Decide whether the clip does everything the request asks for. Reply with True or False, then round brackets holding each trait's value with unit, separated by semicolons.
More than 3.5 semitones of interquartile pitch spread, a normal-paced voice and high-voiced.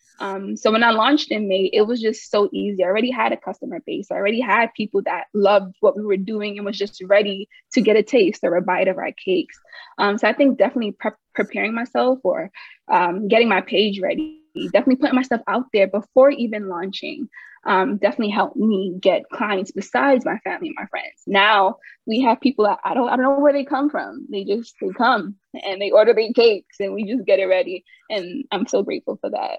False (4.3 semitones; 225 wpm; 215 Hz)